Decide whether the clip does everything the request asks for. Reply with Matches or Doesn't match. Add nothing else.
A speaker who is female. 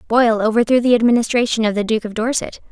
Matches